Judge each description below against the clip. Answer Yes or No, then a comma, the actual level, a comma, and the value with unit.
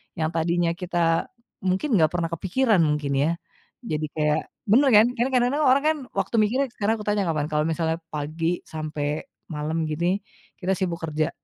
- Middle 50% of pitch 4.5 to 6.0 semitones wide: Yes, average, 5.1 semitones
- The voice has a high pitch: No, medium, 170 Hz